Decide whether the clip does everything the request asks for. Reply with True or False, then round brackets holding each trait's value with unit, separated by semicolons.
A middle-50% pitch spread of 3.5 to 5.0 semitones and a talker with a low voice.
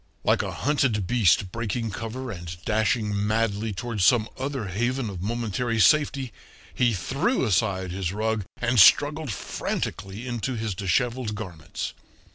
True (3.9 semitones; 110 Hz)